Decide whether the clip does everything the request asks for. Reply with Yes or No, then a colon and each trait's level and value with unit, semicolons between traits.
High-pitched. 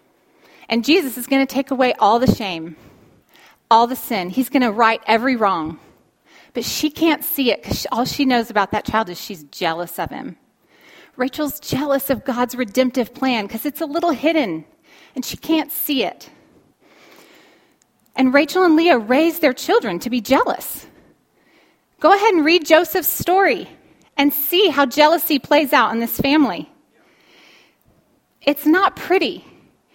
Yes: very high, 275 Hz